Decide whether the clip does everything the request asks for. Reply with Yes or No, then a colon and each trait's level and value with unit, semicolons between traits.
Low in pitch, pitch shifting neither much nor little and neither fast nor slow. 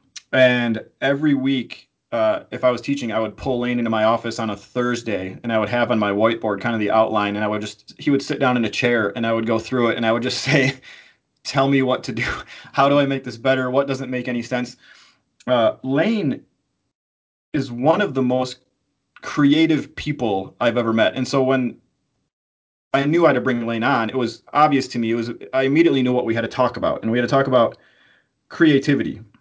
No: low, 125 Hz; average, 3.1 semitones; fast, 230 wpm